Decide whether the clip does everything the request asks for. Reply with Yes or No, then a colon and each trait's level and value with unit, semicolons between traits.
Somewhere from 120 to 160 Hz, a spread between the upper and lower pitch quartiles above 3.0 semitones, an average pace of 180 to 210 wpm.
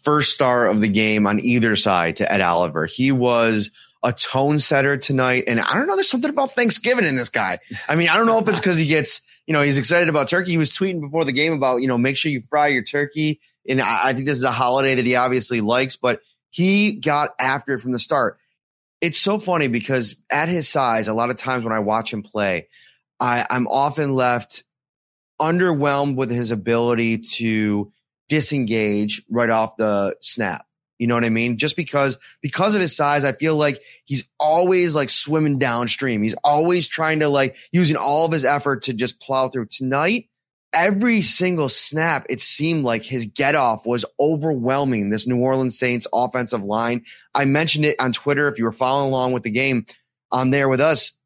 Yes: low, 135 Hz; average, 4.1 semitones; fast, 205 wpm